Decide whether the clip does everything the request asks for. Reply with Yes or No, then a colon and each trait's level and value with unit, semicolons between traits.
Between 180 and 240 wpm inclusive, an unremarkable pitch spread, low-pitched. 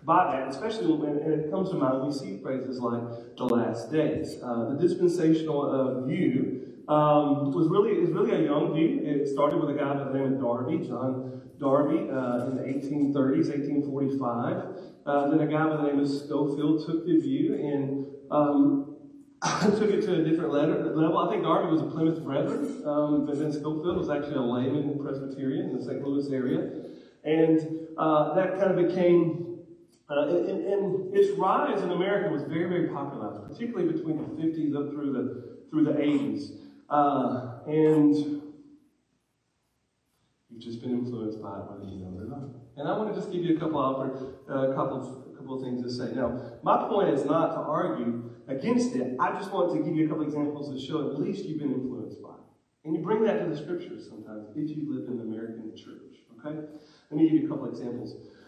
No: fast, 205 wpm; average, 3.7 semitones; medium, 150 Hz